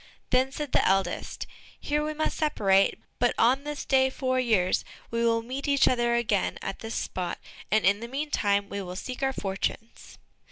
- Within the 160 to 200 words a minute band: Yes, average, 185 wpm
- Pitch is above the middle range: Yes, high, 235 Hz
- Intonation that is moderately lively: Yes, average, 5.0 semitones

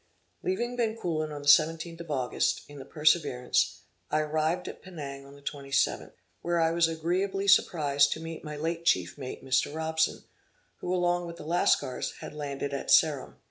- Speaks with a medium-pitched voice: Yes, medium, 155 Hz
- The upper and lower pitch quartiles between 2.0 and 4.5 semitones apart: Yes, average, 3.1 semitones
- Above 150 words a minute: Yes, average, 175 wpm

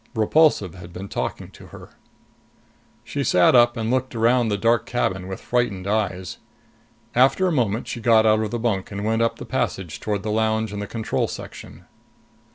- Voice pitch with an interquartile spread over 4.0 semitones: No, average, 3.1 semitones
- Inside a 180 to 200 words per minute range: Yes, average, 185 wpm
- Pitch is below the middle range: Yes, low, 110 Hz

